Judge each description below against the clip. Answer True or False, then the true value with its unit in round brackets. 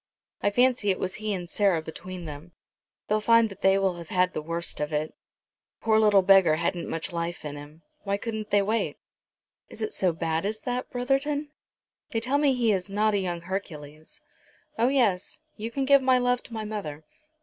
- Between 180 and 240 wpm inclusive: True (205 wpm)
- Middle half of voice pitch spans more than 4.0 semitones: True (5.2 semitones)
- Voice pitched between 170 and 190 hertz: False (200 Hz)